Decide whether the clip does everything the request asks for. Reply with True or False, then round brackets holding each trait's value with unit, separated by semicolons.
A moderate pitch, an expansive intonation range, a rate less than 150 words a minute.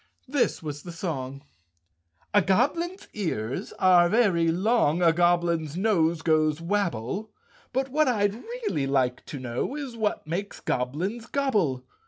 True (175 Hz; 6.8 semitones; 140 wpm)